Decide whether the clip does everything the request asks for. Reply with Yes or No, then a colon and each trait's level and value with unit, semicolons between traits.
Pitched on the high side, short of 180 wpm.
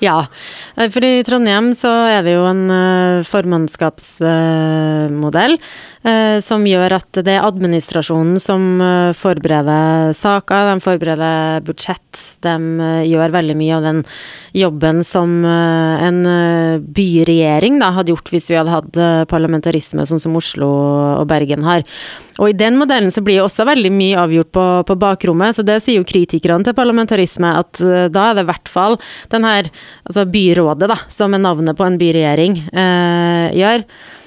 No: medium, 175 Hz; average, 145 wpm